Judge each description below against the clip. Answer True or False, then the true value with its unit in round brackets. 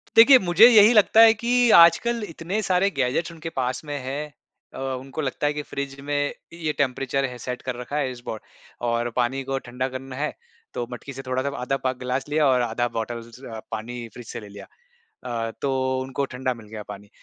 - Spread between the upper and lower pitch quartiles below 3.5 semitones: False (4.0 semitones)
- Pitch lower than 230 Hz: True (135 Hz)